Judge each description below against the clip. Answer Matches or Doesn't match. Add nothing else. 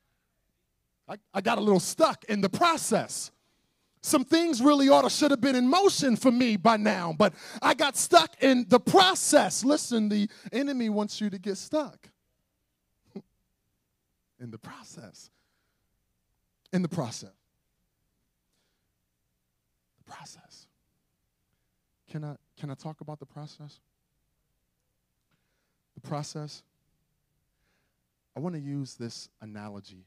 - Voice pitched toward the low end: Doesn't match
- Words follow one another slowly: Matches